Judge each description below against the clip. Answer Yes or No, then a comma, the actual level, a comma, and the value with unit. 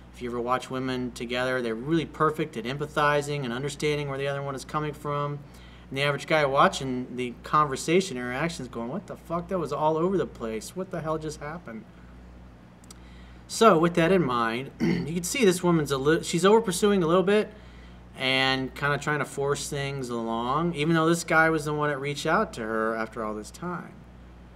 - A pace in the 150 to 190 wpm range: No, fast, 205 wpm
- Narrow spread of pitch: No, average, 5.2 semitones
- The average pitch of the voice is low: No, medium, 145 Hz